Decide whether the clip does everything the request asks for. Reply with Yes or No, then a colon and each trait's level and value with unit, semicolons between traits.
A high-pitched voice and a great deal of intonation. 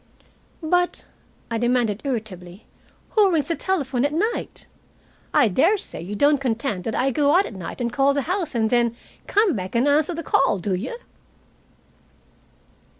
Yes: very high, 265 Hz; wide, 6.2 semitones